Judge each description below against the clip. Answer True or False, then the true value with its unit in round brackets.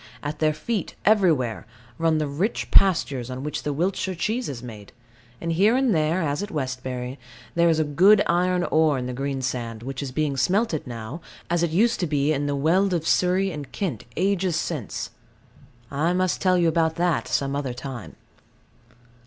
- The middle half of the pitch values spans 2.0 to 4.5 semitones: False (4.9 semitones)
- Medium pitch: True (155 Hz)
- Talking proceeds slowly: False (180 wpm)